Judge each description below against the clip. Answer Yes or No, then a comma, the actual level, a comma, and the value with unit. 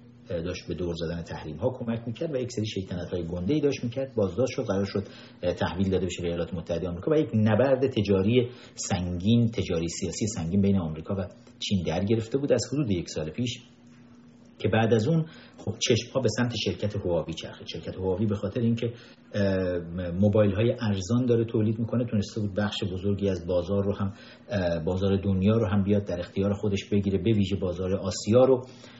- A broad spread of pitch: No, average, 4.3 semitones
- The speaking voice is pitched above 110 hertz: No, low, 105 Hz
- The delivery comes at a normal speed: No, fast, 190 wpm